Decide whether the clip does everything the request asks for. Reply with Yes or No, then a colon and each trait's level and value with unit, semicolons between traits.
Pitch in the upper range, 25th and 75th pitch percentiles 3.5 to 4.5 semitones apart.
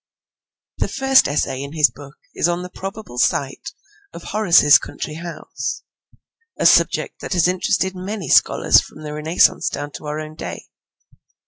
No: medium, 160 Hz; average, 3.9 semitones